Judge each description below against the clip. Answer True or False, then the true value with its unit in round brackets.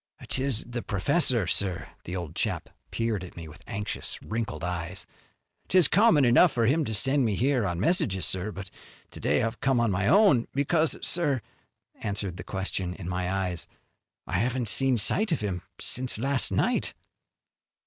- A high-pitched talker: False (110 Hz)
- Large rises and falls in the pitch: True (6.4 semitones)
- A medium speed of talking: True (170 wpm)